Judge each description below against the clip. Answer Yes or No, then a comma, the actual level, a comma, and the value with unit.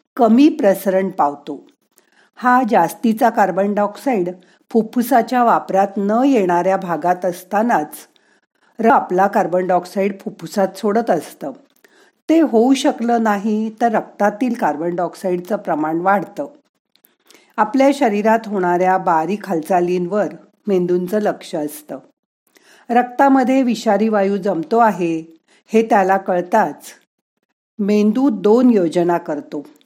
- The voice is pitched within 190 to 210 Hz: Yes, high, 205 Hz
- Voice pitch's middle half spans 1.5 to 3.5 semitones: No, average, 4.4 semitones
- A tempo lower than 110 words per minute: Yes, average, 100 wpm